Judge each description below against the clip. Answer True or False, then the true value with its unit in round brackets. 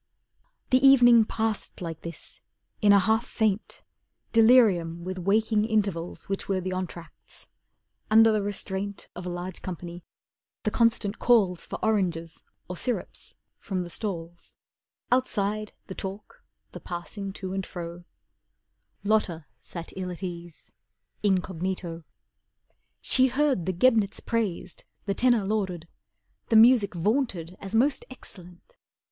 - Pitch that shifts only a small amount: False (3.8 semitones)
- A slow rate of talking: True (130 wpm)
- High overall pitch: True (195 Hz)